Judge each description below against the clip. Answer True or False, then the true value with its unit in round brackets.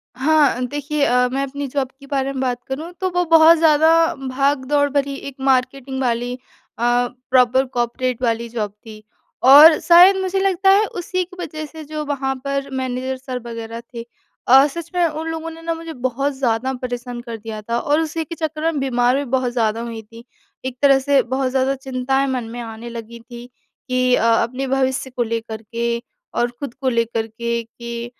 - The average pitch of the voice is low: False (260 Hz)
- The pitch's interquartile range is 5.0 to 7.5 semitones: False (3.3 semitones)